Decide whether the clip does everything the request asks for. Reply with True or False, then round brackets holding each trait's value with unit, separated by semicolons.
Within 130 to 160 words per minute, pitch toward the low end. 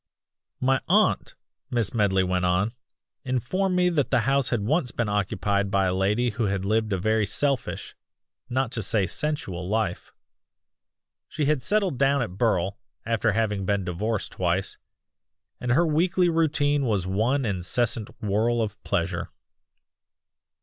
True (145 wpm; 110 Hz)